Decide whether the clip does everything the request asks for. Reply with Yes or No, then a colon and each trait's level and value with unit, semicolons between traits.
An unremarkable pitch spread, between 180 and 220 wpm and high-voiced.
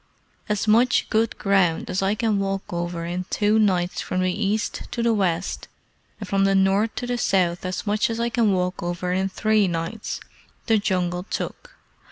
Yes: average, 3.1 semitones; average, 190 wpm; high, 195 Hz